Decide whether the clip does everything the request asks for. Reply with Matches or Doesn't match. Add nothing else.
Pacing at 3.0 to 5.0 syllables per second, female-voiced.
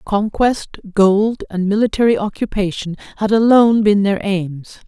Matches